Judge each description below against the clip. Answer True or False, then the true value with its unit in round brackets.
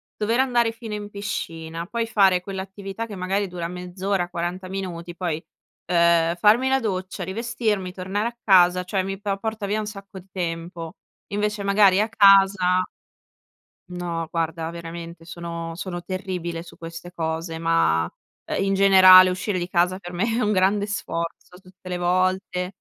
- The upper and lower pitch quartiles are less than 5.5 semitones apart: True (2.7 semitones)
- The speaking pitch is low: False (185 Hz)